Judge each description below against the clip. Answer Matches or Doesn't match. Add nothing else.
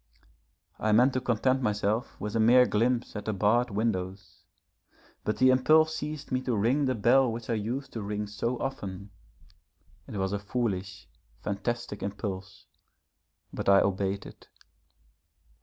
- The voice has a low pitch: Matches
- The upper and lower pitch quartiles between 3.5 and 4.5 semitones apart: Matches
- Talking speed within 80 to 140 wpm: Doesn't match